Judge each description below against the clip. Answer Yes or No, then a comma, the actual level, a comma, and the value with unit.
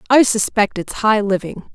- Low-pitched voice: No, high, 215 Hz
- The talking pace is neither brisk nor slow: Yes, average, 170 wpm